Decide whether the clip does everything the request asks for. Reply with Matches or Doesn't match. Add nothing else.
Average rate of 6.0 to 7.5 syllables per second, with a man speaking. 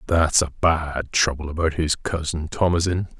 Doesn't match